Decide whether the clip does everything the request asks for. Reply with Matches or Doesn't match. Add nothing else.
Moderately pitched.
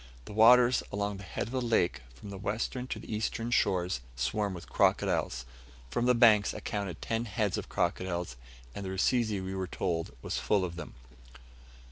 Doesn't match